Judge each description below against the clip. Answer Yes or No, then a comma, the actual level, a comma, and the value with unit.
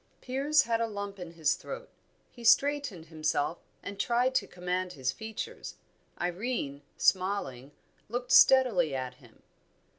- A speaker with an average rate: No, slow, 130 wpm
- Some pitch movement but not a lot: No, wide, 7.3 semitones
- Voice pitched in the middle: No, high, 195 Hz